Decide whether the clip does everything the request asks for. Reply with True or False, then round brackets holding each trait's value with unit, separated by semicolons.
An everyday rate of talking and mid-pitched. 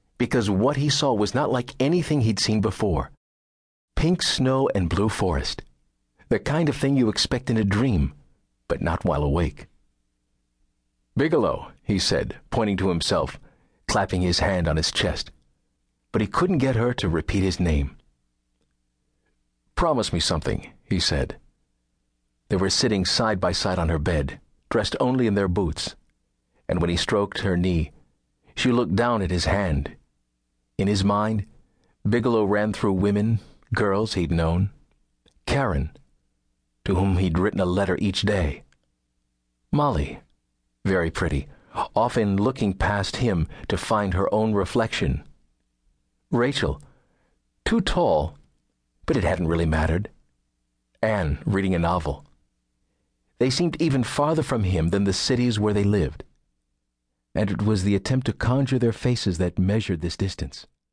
False (145 wpm; 90 Hz)